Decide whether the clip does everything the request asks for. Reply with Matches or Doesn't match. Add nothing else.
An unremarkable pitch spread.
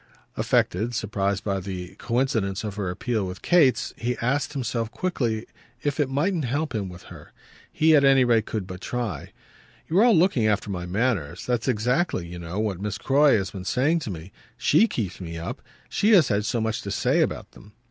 Doesn't match